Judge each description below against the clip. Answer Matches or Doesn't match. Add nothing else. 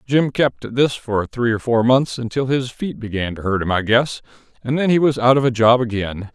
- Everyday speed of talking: Doesn't match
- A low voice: Matches